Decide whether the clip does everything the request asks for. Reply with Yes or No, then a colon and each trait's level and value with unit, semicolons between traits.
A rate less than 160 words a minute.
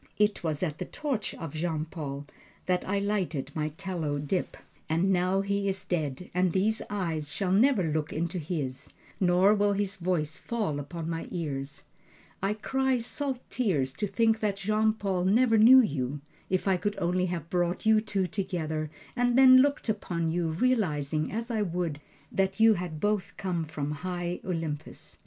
No: average, 175 wpm